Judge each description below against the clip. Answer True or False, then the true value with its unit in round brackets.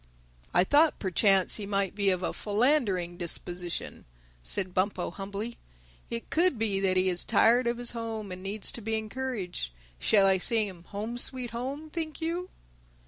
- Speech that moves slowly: False (170 wpm)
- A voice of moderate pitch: False (210 Hz)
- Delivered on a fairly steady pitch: False (4.3 semitones)